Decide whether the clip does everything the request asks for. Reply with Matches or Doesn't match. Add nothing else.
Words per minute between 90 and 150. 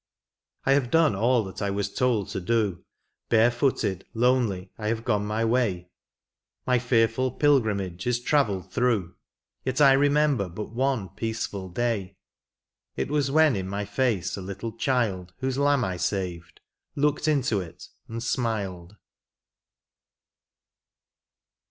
Matches